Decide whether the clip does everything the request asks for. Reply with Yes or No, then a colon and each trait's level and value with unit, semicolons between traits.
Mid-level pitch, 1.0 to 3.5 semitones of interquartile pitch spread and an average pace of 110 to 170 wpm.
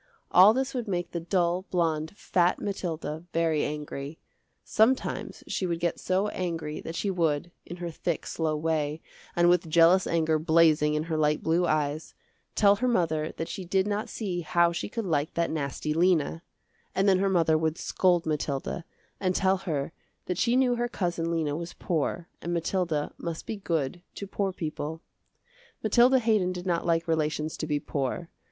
No: medium, 170 Hz; average, 3.1 semitones; average, 180 wpm